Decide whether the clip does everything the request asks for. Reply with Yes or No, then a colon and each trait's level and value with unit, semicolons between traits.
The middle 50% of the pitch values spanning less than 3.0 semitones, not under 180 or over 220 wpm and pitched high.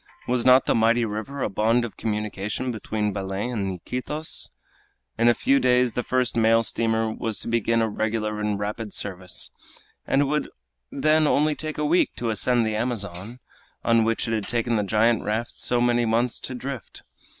No: narrow, 2.6 semitones; average, 185 wpm; low, 115 Hz